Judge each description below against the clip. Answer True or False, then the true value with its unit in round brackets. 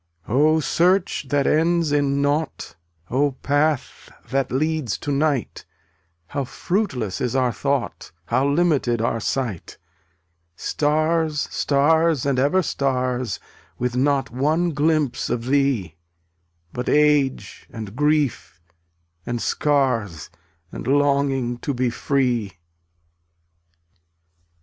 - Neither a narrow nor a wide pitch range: True (3.4 semitones)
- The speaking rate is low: True (110 wpm)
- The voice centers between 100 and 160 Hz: True (140 Hz)